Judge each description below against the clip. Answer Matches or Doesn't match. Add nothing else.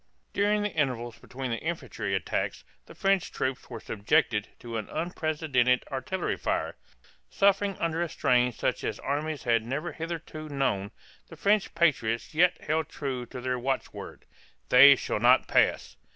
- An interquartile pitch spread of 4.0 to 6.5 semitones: Matches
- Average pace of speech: Matches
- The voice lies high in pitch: Doesn't match